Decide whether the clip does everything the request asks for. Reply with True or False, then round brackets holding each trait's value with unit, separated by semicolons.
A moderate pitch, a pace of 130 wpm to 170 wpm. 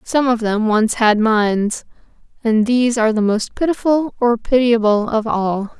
False (230 Hz; 155 wpm)